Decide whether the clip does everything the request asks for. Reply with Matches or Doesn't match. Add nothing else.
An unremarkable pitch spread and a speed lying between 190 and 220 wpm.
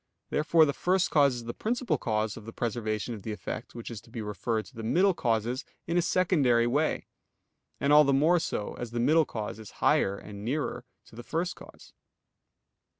Doesn't match